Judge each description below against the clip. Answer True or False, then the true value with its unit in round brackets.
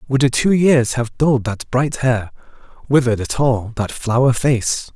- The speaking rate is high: False (180 wpm)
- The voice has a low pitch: True (125 Hz)